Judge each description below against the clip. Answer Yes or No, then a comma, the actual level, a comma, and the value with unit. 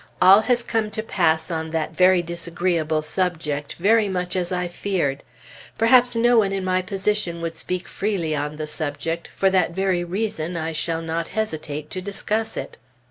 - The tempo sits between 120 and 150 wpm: No, average, 175 wpm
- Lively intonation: No, average, 3.5 semitones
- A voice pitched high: No, medium, 180 Hz